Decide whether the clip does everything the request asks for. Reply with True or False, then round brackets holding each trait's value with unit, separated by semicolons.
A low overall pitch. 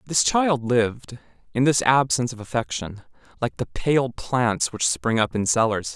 True (120 Hz)